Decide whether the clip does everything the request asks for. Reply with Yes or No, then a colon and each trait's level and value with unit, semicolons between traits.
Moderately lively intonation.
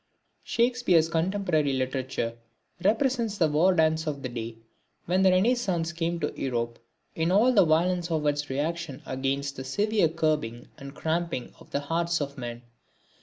Yes: average, 4.8 semitones